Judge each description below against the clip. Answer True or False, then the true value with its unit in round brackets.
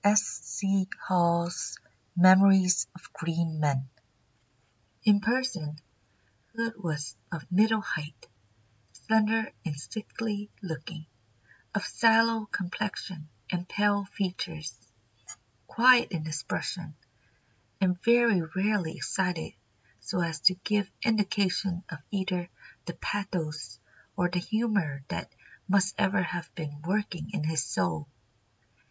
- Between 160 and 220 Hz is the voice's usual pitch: True (185 Hz)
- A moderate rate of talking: False (110 wpm)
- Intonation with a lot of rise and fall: False (4.1 semitones)